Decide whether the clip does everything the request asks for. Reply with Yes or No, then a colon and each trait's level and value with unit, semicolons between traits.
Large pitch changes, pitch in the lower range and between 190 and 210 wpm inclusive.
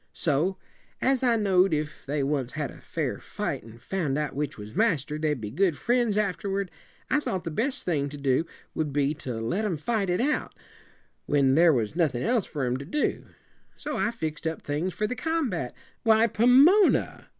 No: wide, 7.2 semitones; medium, 165 Hz; average, 195 wpm